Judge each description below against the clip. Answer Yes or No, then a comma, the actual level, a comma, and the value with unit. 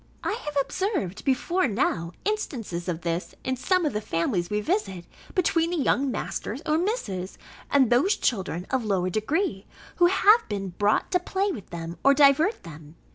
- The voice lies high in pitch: Yes, very high, 255 Hz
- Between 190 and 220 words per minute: No, average, 175 wpm